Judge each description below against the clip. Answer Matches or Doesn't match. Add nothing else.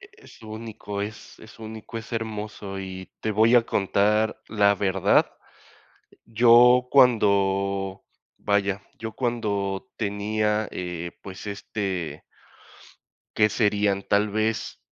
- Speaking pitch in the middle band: Doesn't match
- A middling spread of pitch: Doesn't match